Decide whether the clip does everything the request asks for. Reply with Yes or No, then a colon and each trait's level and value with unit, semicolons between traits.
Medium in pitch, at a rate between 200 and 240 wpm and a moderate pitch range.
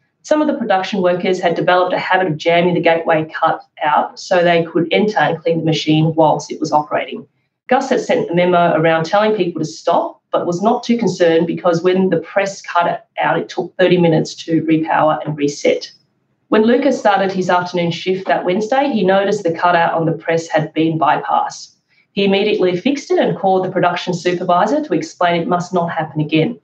Yes: medium, 175 Hz; fast, 205 wpm; average, 3.1 semitones